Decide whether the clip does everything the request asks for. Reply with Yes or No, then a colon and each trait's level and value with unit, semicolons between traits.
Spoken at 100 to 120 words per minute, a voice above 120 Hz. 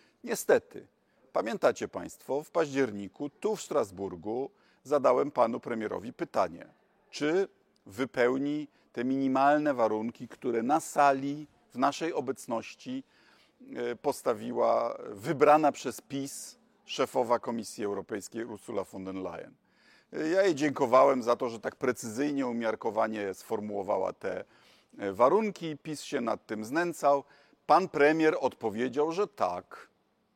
Yes: slow, 110 wpm; low, 135 Hz